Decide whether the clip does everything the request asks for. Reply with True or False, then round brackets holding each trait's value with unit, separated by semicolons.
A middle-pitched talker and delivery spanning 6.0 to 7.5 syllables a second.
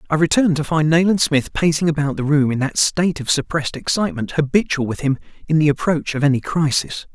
True (155 Hz; 6.2 syllables/s)